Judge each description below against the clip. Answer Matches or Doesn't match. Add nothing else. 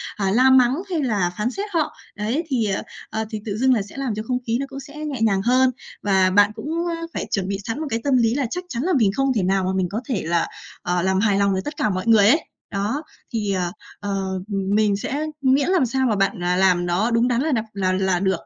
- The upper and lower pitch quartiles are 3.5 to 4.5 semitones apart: Doesn't match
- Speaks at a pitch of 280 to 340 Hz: Doesn't match